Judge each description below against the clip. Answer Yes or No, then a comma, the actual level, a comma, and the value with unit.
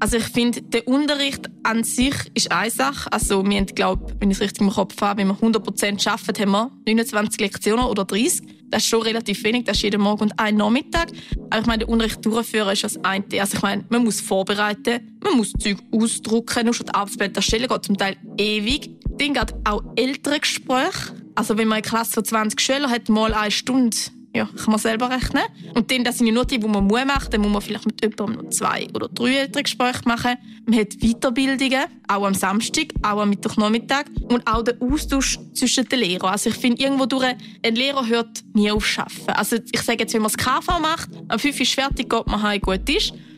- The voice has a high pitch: Yes, high, 225 Hz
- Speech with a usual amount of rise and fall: Yes, average, 3.0 semitones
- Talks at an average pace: No, fast, 230 wpm